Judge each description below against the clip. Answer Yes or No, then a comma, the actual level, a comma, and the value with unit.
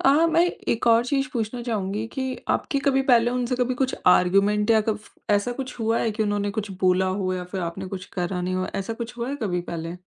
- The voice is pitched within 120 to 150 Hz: No, high, 215 Hz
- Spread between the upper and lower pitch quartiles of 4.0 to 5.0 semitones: Yes, average, 4.4 semitones